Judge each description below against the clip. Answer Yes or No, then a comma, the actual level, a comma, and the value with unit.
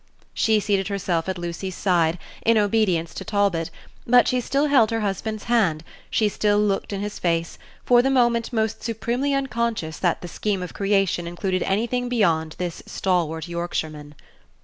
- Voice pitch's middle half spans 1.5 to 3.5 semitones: No, average, 4.8 semitones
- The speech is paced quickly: No, average, 165 wpm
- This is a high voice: Yes, high, 200 Hz